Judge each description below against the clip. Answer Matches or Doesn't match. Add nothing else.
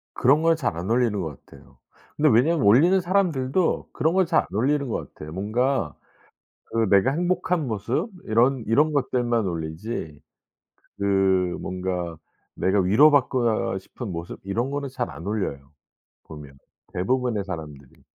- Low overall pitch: Matches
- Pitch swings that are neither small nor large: Doesn't match